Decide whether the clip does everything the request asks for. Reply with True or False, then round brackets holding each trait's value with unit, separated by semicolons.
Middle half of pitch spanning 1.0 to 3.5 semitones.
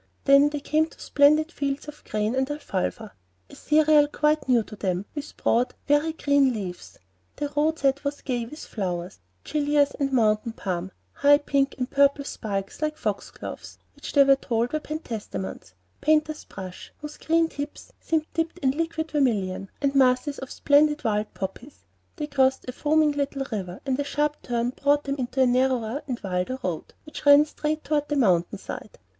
False (4.6 semitones)